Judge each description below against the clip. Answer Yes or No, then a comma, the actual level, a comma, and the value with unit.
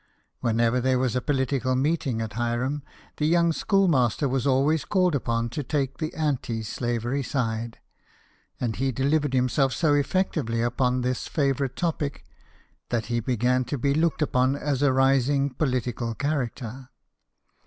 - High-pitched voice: No, low, 130 Hz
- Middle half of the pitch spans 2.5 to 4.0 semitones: Yes, average, 3.2 semitones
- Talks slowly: No, average, 145 wpm